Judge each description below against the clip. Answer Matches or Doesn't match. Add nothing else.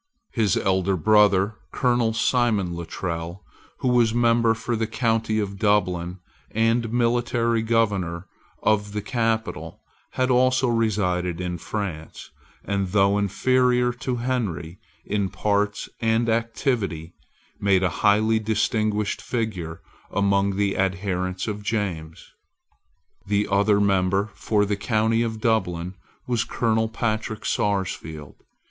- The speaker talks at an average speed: Doesn't match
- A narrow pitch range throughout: Doesn't match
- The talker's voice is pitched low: Matches